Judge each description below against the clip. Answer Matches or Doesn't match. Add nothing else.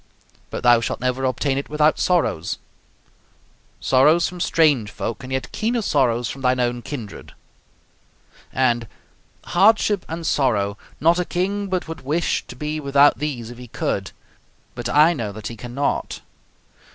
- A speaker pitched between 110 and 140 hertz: Matches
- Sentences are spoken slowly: Doesn't match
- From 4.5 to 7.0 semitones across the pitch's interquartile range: Matches